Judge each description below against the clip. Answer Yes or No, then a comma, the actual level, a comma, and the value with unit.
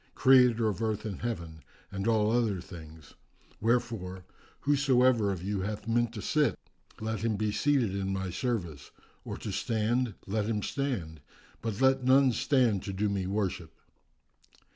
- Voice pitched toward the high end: No, low, 110 Hz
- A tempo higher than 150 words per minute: Yes, average, 160 wpm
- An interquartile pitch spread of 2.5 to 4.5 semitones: Yes, average, 3.9 semitones